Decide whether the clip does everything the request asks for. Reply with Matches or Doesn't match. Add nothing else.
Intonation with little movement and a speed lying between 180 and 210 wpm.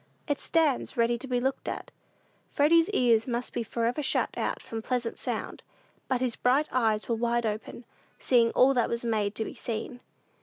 Matches